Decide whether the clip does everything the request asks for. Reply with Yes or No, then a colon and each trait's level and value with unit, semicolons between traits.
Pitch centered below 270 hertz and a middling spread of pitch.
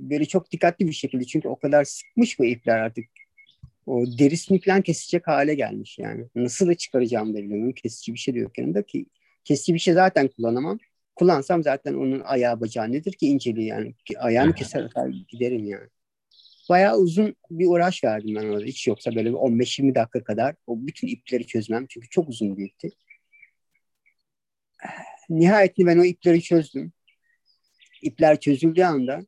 No: medium, 140 Hz; wide, 6.9 semitones